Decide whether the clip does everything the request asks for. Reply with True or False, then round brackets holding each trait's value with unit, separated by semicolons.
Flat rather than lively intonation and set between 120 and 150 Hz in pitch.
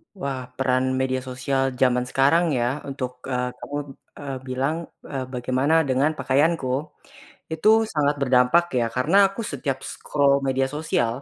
True (2.1 semitones; 135 Hz)